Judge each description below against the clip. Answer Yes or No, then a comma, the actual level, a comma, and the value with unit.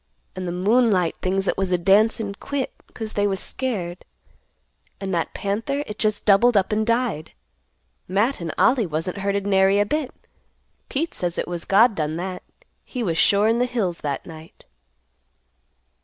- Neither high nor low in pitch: No, high, 200 Hz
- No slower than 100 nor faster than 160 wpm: No, average, 170 wpm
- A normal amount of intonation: Yes, average, 4.0 semitones